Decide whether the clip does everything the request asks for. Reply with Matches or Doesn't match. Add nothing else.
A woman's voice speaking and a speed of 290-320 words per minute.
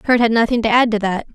Matches